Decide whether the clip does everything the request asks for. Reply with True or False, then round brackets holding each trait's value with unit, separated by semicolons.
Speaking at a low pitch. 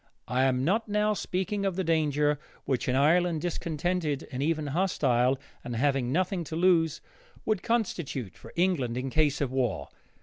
False (155 Hz)